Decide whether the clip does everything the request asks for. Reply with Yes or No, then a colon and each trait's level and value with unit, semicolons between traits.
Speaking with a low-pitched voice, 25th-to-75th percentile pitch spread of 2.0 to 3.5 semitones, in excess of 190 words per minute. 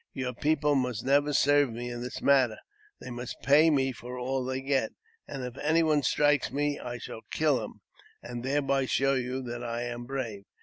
Yes: low, 130 Hz; average, 2.7 semitones; average, 200 wpm